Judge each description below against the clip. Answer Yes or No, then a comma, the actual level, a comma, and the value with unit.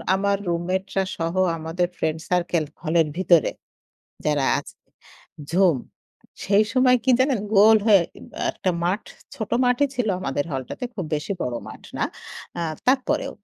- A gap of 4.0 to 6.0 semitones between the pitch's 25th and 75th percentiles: Yes, average, 4.8 semitones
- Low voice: No, medium, 185 Hz